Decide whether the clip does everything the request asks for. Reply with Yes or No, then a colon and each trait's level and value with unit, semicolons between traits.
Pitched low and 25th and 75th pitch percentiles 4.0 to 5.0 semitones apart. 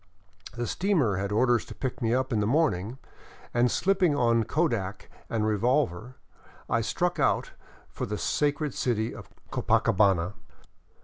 Yes: low, 120 Hz; average, 4.4 semitones